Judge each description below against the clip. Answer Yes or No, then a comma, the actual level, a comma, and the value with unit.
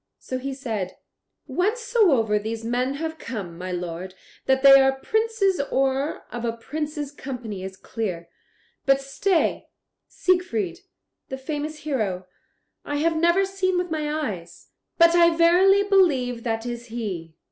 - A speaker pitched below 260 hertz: No, very high, 270 Hz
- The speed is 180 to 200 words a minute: No, average, 140 wpm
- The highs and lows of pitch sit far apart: Yes, wide, 7.0 semitones